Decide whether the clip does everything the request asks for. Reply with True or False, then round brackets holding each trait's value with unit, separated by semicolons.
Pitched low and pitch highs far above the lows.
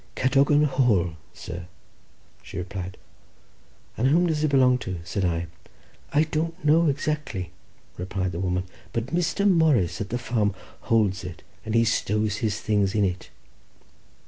True (110 Hz; 7.8 semitones)